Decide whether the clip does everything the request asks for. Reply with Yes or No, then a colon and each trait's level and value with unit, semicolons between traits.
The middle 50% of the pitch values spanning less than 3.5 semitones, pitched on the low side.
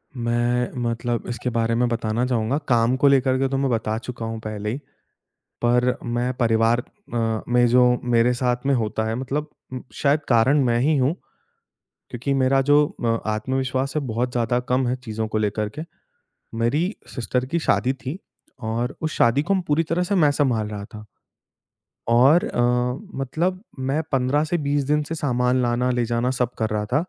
Yes: average, 2.8 semitones; low, 125 Hz